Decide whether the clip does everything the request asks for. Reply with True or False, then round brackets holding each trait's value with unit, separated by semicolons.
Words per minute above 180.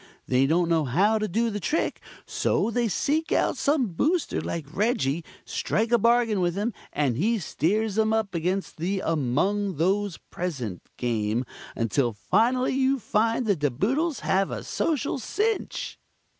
False (155 wpm)